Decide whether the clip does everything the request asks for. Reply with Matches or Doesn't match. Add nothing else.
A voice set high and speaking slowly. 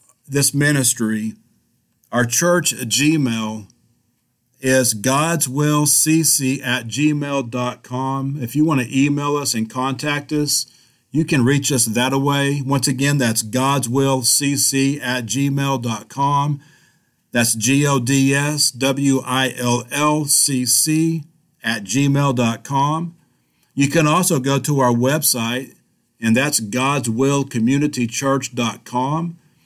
Doesn't match